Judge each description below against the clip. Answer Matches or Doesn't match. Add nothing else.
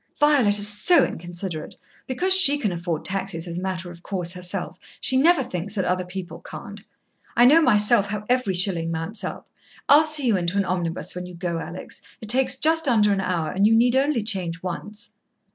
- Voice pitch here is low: Doesn't match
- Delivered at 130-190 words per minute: Doesn't match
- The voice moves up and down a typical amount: Doesn't match